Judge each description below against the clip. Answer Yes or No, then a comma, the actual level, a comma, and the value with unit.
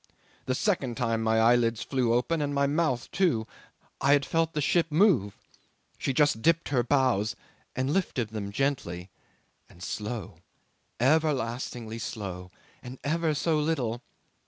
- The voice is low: Yes, low, 130 Hz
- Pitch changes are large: No, average, 5.0 semitones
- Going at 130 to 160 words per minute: Yes, average, 140 wpm